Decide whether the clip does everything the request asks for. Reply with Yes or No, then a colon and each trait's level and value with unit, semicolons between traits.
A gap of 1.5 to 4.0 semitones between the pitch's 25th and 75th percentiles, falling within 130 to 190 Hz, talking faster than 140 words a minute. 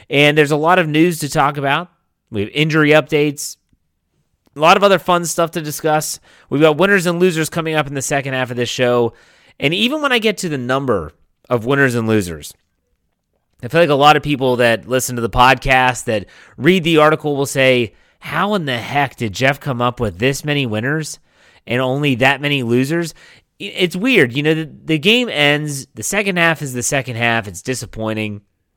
No: average, 4.4 semitones; medium, 140 Hz; fast, 205 wpm